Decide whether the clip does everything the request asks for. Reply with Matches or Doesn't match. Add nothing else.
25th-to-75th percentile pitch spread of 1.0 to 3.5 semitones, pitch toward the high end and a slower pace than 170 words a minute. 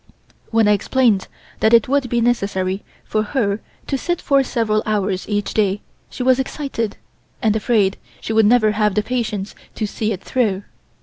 Doesn't match